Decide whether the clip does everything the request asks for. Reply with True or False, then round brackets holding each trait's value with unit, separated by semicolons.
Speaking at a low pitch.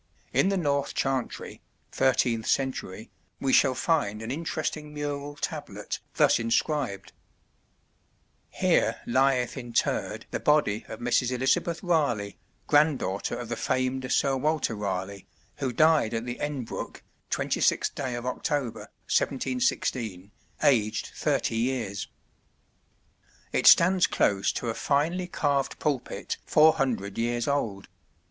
True (130 Hz)